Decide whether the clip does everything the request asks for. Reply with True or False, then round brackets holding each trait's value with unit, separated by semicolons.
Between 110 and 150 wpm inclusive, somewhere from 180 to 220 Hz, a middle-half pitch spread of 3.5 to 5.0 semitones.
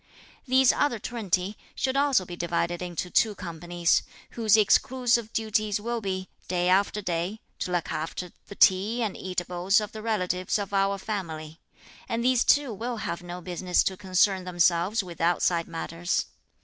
False (160 wpm; 190 Hz; 3.8 semitones)